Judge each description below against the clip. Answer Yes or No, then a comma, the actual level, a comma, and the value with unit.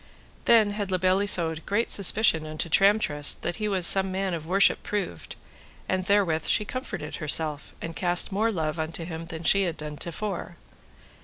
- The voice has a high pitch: No, medium, 180 Hz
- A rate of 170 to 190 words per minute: Yes, average, 180 wpm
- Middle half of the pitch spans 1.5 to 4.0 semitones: Yes, average, 3.7 semitones